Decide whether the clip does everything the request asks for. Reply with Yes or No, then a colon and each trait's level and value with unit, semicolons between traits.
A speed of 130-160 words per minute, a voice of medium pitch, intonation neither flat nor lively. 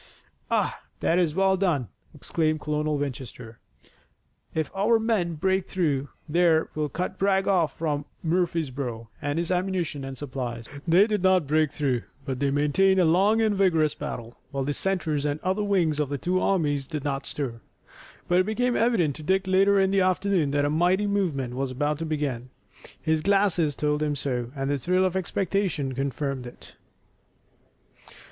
No: average, 170 wpm; medium, 155 Hz; average, 5.0 semitones